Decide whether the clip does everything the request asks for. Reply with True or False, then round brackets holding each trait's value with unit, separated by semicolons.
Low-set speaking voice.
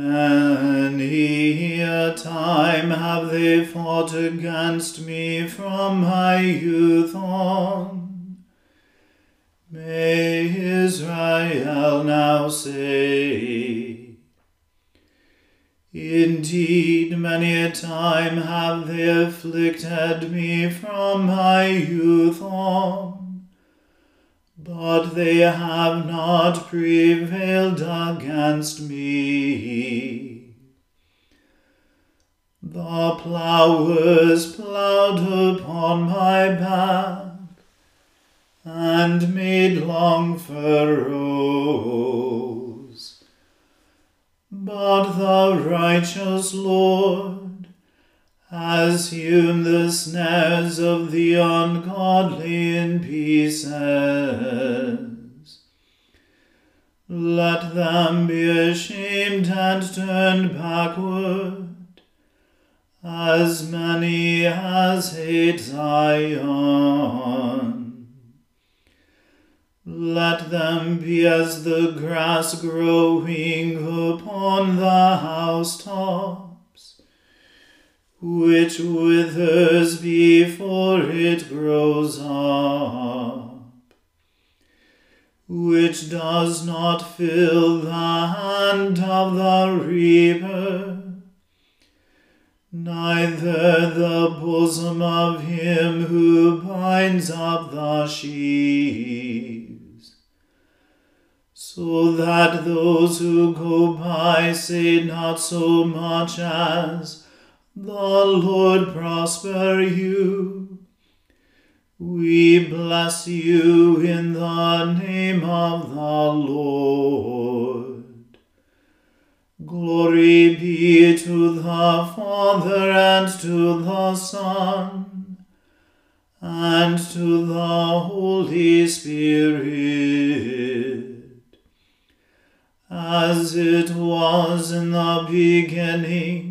False (170 Hz)